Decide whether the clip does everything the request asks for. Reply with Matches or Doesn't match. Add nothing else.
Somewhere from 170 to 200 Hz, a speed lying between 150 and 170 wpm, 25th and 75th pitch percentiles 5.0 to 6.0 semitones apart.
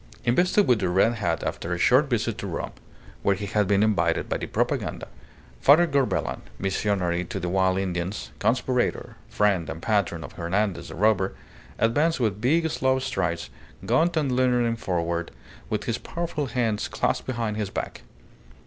Doesn't match